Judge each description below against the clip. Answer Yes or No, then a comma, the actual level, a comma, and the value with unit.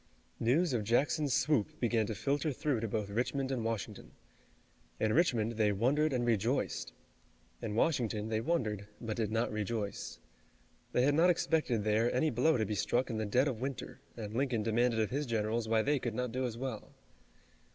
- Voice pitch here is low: Yes, low, 115 Hz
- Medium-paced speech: Yes, average, 185 wpm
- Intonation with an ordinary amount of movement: Yes, average, 3.5 semitones